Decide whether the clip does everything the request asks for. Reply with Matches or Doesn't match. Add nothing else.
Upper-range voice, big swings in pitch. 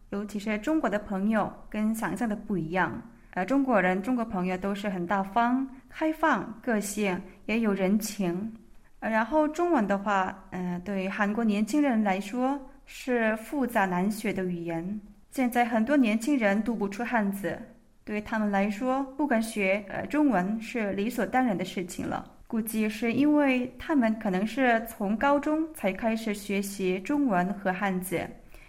Doesn't match